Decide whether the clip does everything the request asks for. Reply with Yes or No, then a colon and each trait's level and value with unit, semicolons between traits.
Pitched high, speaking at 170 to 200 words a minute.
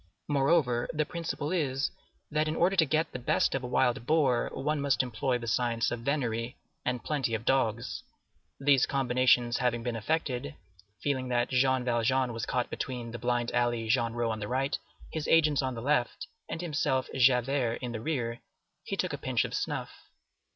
No: low, 125 Hz; average, 180 wpm